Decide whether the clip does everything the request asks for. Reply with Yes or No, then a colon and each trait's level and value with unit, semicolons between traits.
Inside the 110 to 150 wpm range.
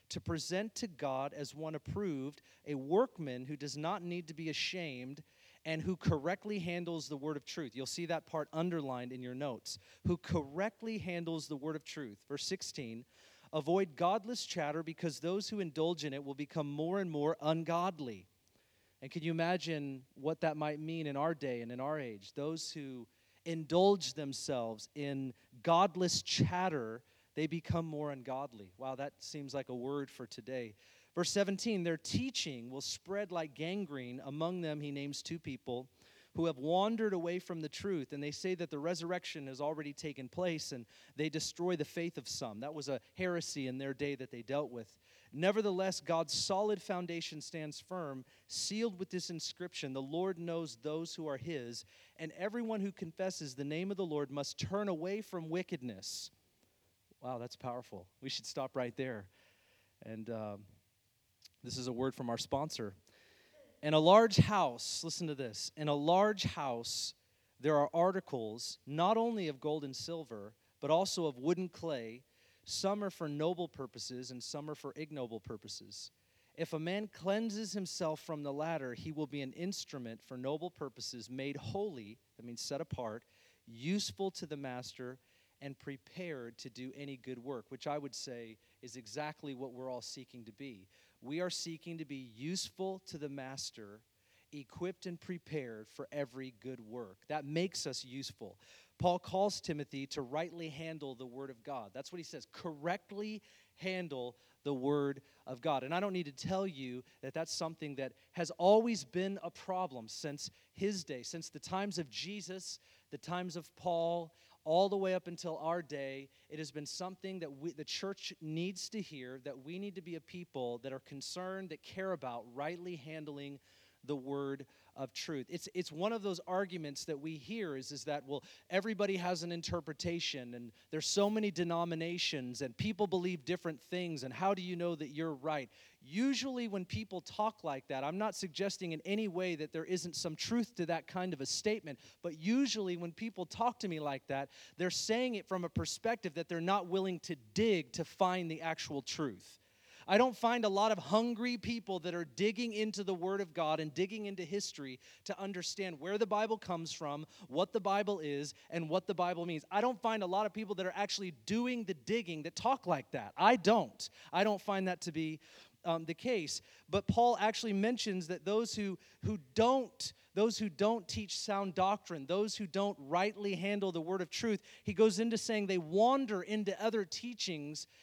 No: average, 185 wpm